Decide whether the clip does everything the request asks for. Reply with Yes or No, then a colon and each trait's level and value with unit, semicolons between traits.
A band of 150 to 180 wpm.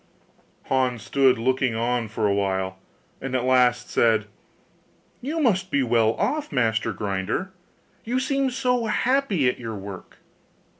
No: average, 140 wpm